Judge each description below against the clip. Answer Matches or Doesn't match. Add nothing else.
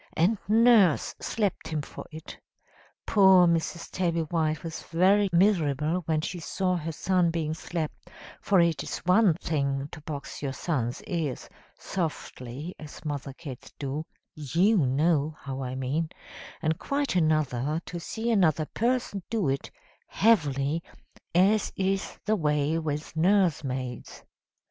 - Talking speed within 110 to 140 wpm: Matches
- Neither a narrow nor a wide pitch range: Matches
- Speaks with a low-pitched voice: Doesn't match